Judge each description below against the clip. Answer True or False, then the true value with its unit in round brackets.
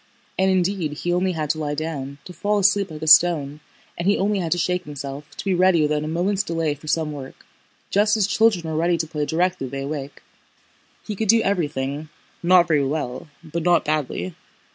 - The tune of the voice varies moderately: True (3.8 semitones)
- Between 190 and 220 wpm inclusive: True (205 wpm)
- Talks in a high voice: False (165 Hz)